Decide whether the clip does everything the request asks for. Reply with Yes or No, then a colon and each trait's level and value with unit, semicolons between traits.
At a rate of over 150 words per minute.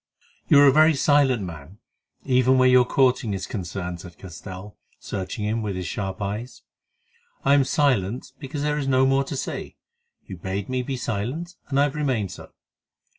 Yes: average, 180 wpm